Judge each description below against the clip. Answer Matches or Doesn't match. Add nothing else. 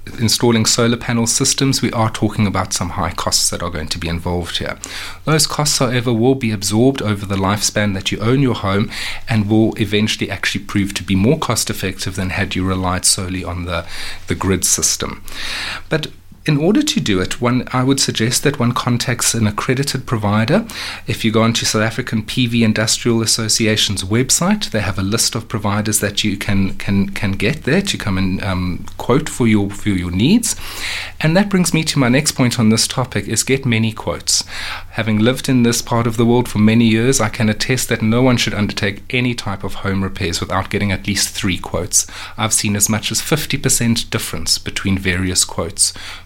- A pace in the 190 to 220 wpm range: Matches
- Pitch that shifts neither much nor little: Matches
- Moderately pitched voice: Doesn't match